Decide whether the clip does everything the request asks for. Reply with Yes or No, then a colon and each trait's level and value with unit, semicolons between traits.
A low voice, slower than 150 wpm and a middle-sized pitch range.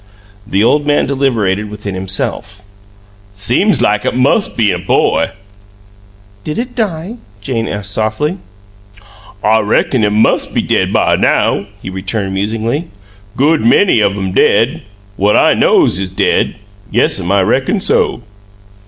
No: low, 110 Hz; average, 140 wpm; wide, 6.3 semitones